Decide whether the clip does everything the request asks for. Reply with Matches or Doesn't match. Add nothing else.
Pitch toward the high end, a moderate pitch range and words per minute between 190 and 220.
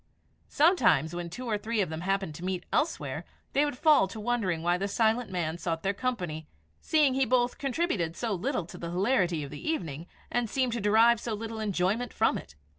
Doesn't match